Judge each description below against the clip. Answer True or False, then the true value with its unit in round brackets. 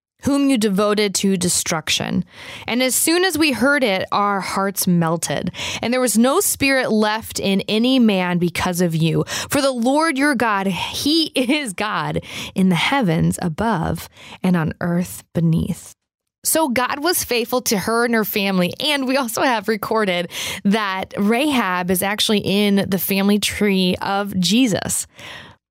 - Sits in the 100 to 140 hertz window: False (205 Hz)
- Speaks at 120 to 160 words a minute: True (155 wpm)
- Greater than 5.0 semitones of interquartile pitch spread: True (5.4 semitones)